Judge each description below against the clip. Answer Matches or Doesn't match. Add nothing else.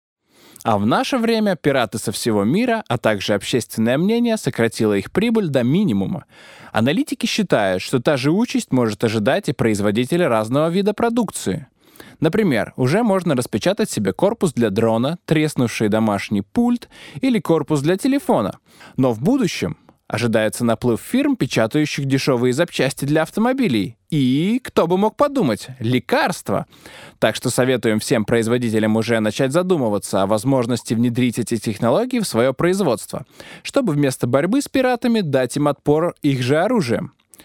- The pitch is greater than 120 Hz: Matches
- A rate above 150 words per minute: Doesn't match